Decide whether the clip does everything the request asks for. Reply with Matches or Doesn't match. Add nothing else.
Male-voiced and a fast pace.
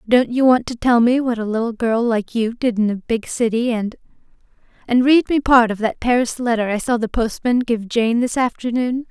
Doesn't match